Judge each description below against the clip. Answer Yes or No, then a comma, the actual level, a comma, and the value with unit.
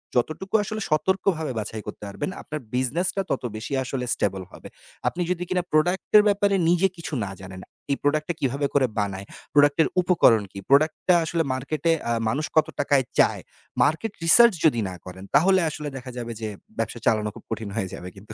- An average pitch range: No, wide, 7.2 semitones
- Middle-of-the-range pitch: Yes, medium, 145 Hz